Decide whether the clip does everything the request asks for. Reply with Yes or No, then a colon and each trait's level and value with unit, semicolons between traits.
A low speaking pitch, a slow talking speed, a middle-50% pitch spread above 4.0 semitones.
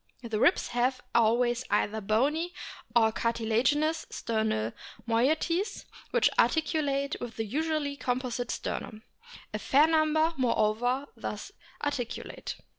No: very high, 250 Hz; slow, 110 wpm; average, 5.1 semitones